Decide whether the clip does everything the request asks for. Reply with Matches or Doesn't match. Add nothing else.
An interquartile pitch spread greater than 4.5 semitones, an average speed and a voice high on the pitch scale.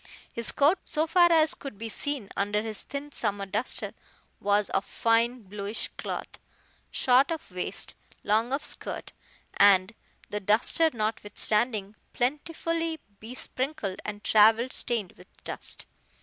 Doesn't match